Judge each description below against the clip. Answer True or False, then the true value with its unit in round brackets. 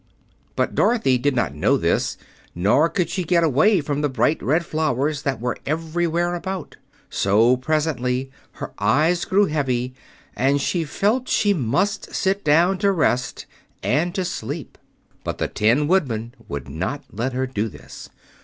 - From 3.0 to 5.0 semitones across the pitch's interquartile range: False (5.6 semitones)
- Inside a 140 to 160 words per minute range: True (155 wpm)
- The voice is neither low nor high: True (145 Hz)